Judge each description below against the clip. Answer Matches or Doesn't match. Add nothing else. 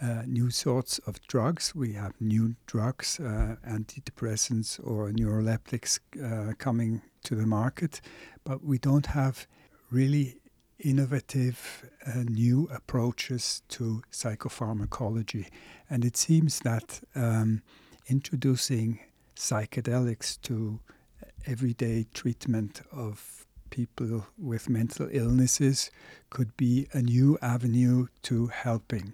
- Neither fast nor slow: Doesn't match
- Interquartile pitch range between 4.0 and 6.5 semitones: Doesn't match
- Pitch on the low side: Matches